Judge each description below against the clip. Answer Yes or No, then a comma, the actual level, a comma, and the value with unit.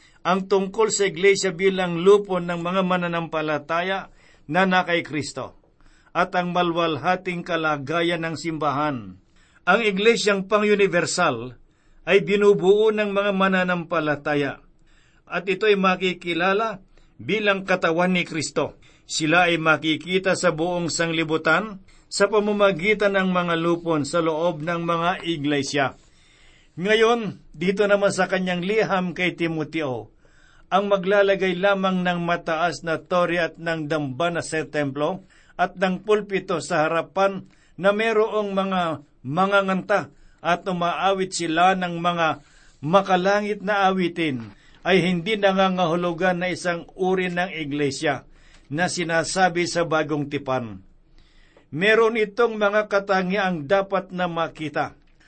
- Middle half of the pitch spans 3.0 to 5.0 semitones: Yes, average, 3.3 semitones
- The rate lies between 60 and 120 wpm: Yes, average, 115 wpm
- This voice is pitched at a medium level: Yes, medium, 175 Hz